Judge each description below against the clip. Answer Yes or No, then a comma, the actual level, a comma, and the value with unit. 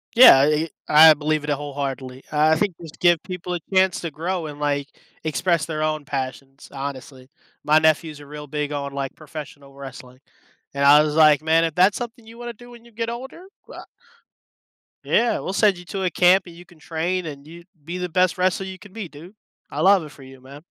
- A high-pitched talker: No, medium, 155 Hz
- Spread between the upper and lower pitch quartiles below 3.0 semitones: No, average, 4.1 semitones